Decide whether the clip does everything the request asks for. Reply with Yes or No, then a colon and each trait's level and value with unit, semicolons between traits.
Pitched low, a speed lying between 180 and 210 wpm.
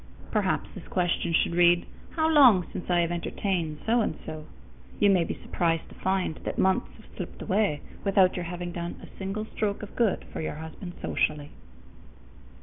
No: medium, 180 Hz; average, 185 wpm